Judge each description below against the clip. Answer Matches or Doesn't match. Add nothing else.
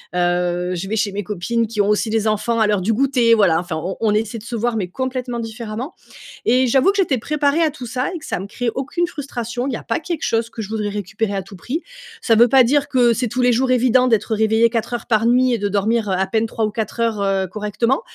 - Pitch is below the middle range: Doesn't match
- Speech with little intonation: Doesn't match